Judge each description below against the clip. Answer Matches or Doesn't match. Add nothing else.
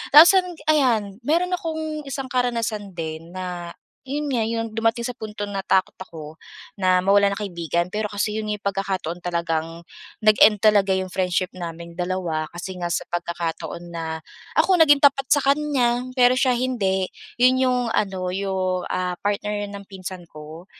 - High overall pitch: Matches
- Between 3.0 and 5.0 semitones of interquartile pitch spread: Doesn't match